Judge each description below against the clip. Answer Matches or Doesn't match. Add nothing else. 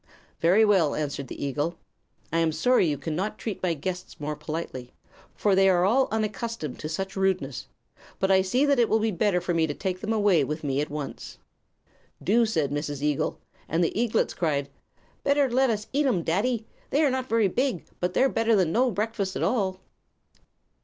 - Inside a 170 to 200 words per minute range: Matches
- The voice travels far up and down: Matches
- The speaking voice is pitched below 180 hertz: Doesn't match